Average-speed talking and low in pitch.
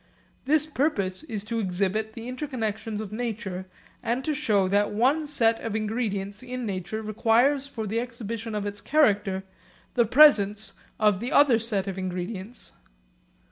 No: average, 150 wpm; high, 220 Hz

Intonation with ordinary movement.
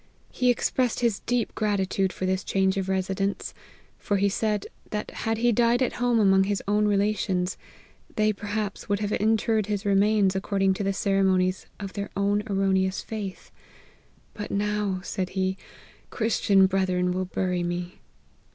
No: narrow, 1.9 semitones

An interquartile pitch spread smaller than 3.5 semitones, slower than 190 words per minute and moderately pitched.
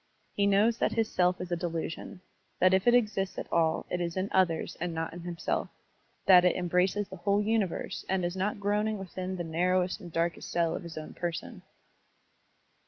No: narrow, 2.5 semitones; average, 195 wpm; medium, 180 Hz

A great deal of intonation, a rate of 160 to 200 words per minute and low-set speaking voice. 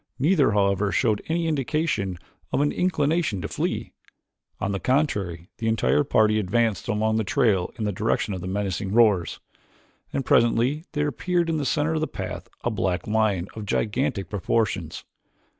Yes: wide, 6.7 semitones; average, 165 wpm; low, 110 Hz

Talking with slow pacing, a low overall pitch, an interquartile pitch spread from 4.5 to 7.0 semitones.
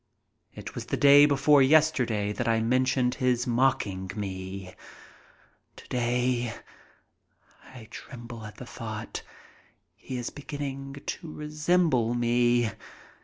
No: slow, 100 wpm; low, 125 Hz; average, 3.3 semitones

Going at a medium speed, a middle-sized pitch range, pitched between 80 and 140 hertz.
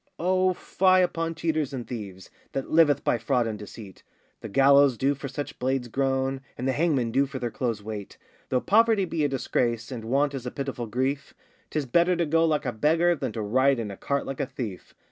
No: fast, 215 wpm; average, 4.5 semitones; low, 135 Hz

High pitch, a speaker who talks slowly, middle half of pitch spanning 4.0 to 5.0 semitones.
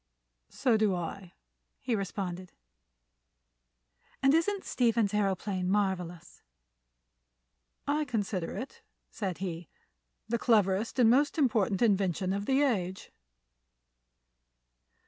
Yes: high, 205 Hz; slow, 95 wpm; average, 4.3 semitones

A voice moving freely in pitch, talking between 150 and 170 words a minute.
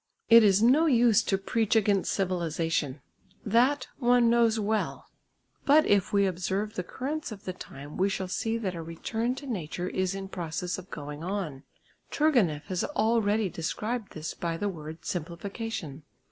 No: average, 5.0 semitones; average, 160 wpm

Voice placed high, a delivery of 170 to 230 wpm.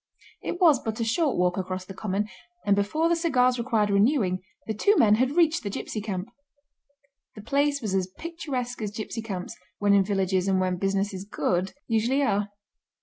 Yes: high, 210 Hz; average, 180 wpm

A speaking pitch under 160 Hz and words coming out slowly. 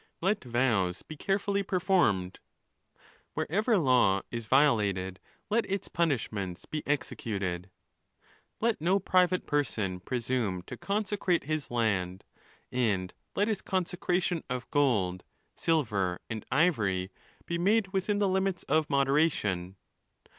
Yes: medium, 140 Hz; slow, 115 wpm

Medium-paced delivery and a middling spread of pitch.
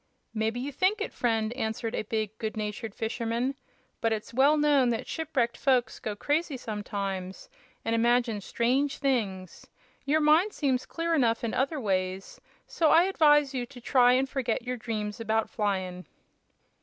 Yes: average, 160 wpm; average, 4.2 semitones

